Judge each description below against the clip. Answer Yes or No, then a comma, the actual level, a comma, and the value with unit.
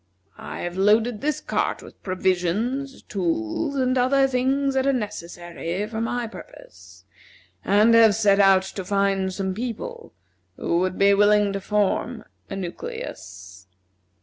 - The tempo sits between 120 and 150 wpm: Yes, average, 140 wpm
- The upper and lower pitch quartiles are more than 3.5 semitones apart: Yes, average, 4.8 semitones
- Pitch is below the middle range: No, high, 205 Hz